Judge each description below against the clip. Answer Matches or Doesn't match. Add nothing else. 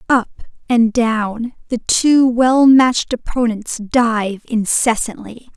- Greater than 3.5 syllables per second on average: Doesn't match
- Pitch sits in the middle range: Doesn't match